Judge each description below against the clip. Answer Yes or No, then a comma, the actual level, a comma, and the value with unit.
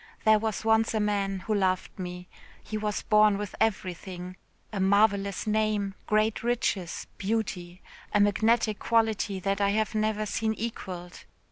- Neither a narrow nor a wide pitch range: No, narrow, 2.1 semitones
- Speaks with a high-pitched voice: Yes, high, 210 Hz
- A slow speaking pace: No, average, 145 wpm